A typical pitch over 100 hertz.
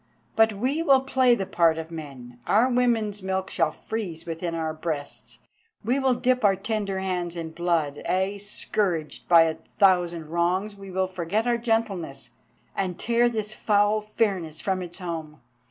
Yes: high, 190 Hz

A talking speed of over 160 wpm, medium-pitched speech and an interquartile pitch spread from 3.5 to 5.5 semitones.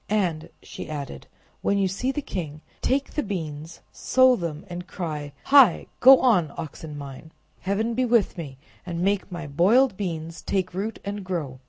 Yes: average, 170 wpm; medium, 180 Hz; average, 5.1 semitones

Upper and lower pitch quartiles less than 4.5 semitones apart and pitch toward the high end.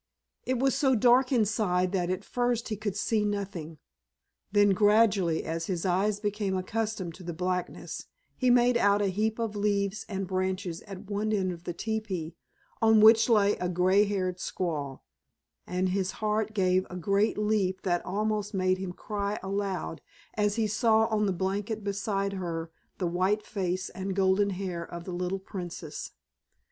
Yes: narrow, 2.6 semitones; high, 200 Hz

